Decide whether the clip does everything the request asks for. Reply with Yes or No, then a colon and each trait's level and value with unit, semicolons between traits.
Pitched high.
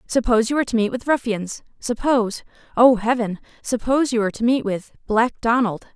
Yes: high, 235 Hz